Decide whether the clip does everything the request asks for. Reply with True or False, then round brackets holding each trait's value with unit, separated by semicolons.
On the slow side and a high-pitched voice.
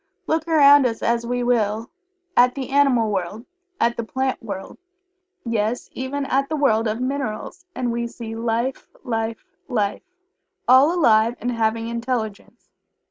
False (145 wpm; 235 Hz)